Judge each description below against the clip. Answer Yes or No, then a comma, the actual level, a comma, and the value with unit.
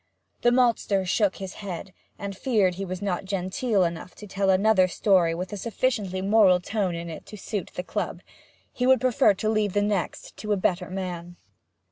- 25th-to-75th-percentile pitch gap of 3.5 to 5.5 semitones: No, average, 2.7 semitones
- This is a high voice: Yes, high, 195 Hz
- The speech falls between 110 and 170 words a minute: No, average, 190 wpm